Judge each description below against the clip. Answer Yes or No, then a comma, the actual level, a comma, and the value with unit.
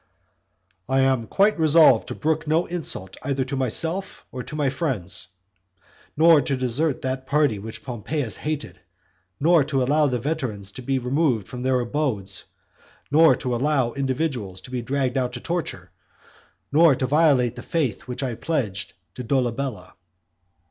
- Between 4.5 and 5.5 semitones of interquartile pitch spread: No, average, 3.7 semitones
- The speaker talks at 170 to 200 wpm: No, average, 155 wpm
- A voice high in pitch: No, low, 135 Hz